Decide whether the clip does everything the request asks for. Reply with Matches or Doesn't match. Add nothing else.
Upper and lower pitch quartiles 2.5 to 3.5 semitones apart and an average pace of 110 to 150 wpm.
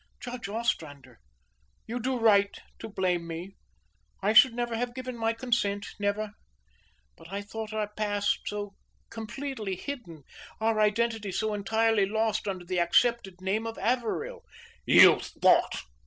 Matches